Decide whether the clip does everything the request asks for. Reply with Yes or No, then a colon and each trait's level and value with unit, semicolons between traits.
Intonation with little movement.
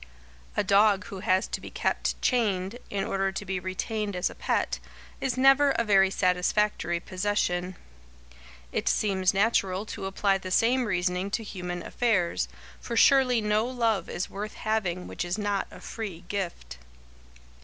No: average, 3.0 semitones